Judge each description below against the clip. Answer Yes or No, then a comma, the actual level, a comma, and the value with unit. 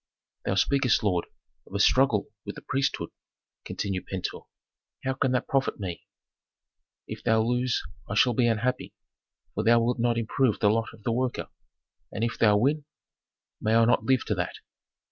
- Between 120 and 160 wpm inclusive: No, average, 170 wpm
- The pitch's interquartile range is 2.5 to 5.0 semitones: Yes, average, 3.3 semitones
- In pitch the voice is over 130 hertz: No, low, 115 Hz